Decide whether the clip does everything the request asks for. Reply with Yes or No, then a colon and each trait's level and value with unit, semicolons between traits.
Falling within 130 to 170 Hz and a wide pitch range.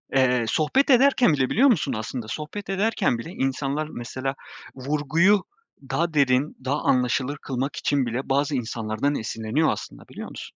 No: medium, 140 Hz; average, 3.8 semitones